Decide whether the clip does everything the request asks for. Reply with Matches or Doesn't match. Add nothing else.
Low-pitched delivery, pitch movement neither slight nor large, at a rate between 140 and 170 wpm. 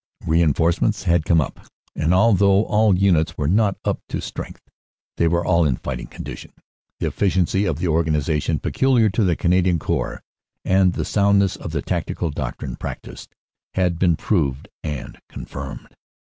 Matches